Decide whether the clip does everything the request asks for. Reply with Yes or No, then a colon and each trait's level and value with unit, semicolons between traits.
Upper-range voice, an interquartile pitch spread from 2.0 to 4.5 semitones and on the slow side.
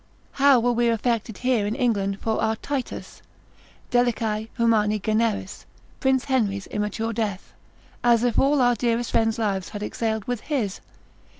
No: high, 230 Hz; narrow, 2.5 semitones; average, 145 wpm